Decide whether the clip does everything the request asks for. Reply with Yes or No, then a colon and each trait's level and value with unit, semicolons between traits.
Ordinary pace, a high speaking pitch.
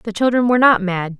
No: fast, 250 wpm; high, 215 Hz